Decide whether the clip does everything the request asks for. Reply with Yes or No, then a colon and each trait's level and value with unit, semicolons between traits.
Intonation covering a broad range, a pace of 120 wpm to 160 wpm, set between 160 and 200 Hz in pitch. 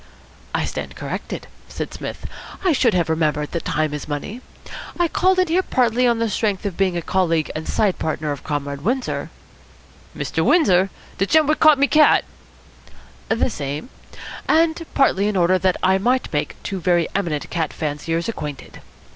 No: wide, 8.0 semitones; average, 175 wpm; high, 190 Hz